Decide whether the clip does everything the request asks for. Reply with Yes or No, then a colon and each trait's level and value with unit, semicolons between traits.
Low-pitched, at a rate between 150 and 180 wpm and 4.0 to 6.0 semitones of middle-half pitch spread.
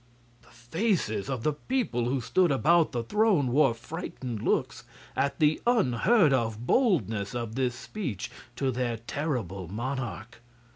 No: low, 130 Hz; average, 140 wpm; wide, 5.5 semitones